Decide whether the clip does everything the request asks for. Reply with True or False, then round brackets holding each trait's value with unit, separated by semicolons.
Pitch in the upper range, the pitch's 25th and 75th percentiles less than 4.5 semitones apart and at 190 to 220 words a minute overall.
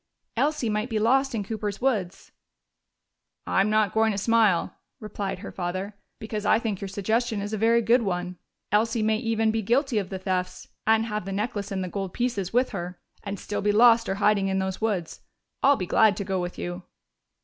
True (210 Hz; 2.7 semitones; 205 wpm)